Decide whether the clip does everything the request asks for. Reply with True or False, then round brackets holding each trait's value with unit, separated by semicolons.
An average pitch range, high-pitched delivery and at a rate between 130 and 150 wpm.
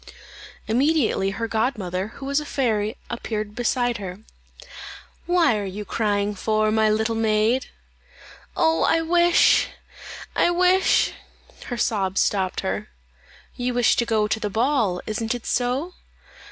True (3.9 semitones; 225 Hz; 140 wpm)